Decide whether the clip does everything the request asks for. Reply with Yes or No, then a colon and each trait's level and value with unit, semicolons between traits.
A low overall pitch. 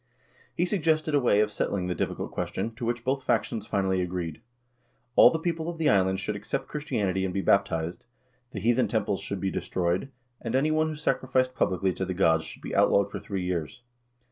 Yes: low, 105 Hz